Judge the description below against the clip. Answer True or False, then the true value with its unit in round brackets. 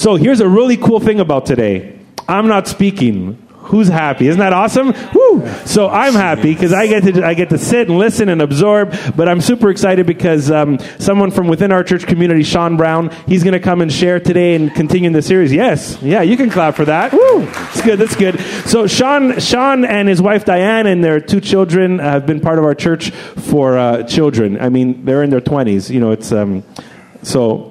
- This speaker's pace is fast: True (215 wpm)